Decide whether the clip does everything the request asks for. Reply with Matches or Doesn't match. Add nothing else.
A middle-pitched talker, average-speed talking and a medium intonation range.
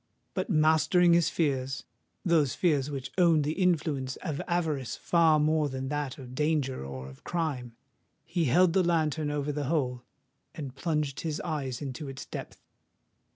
Matches